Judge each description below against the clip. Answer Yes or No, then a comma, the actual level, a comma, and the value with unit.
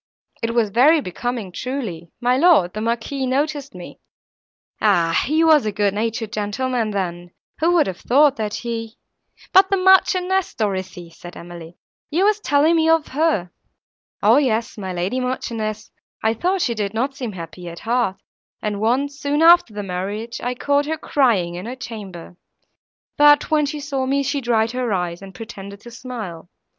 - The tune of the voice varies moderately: No, wide, 6.2 semitones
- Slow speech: No, average, 170 wpm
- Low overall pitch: No, high, 235 Hz